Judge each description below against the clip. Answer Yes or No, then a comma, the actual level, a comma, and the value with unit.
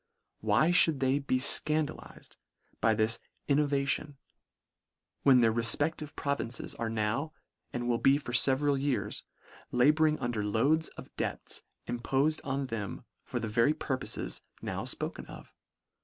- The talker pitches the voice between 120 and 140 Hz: Yes, low, 135 Hz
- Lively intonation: No, average, 4.0 semitones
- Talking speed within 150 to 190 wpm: No, average, 140 wpm